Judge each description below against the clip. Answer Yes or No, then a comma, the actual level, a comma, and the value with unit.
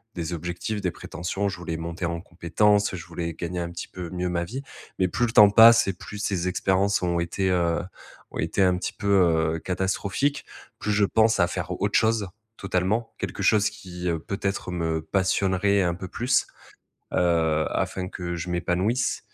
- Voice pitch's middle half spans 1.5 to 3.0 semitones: Yes, average, 2.7 semitones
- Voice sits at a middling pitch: No, very low, 90 Hz